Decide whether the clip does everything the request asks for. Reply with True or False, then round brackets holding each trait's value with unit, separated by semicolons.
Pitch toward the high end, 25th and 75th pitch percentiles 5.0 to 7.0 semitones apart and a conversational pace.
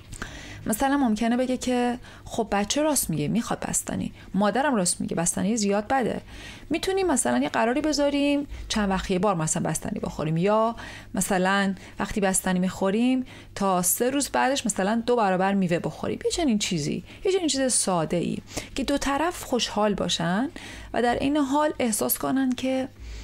False (230 Hz; 5.6 semitones; 160 wpm)